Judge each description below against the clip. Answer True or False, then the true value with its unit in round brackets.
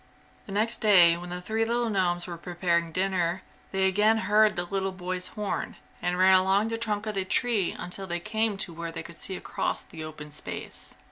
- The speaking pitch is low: False (190 Hz)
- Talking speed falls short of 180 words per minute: False (205 wpm)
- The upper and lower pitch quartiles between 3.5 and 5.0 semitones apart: False (3.1 semitones)